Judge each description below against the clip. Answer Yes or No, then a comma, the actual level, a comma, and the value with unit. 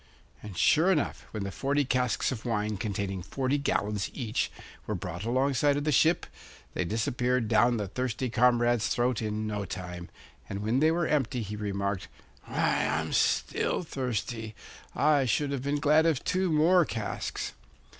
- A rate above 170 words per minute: No, average, 165 wpm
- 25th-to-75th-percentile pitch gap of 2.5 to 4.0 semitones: No, average, 5.1 semitones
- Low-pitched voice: Yes, low, 120 Hz